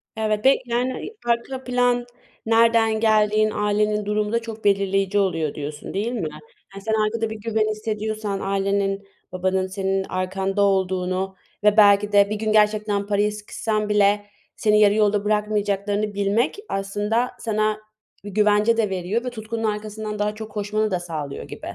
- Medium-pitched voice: No, high, 210 Hz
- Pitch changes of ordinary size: No, narrow, 1.6 semitones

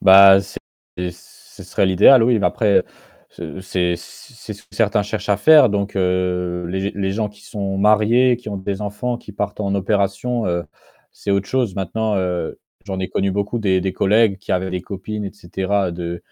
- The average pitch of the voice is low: Yes, low, 100 Hz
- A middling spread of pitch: No, narrow, 2.1 semitones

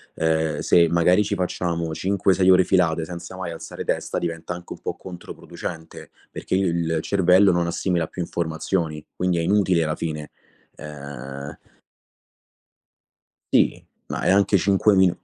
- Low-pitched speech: Yes, very low, 85 Hz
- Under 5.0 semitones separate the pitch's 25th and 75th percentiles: Yes, narrow, 2.4 semitones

